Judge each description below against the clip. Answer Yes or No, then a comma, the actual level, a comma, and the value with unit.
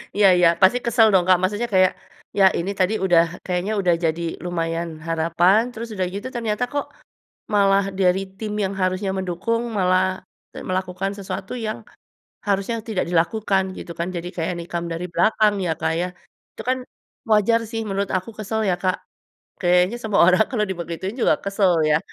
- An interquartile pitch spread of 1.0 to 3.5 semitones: Yes, average, 3.0 semitones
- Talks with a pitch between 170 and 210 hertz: Yes, high, 190 Hz